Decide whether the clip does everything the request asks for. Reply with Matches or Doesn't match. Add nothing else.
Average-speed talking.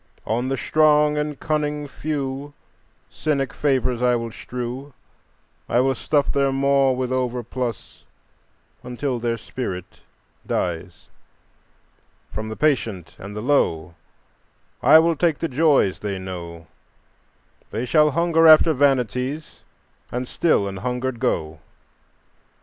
Doesn't match